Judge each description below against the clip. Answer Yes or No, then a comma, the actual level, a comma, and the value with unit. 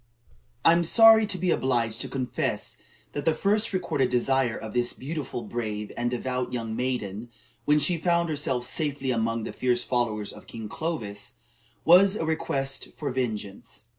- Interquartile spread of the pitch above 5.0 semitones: Yes, wide, 5.6 semitones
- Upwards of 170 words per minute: No, average, 165 wpm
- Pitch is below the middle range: Yes, low, 130 Hz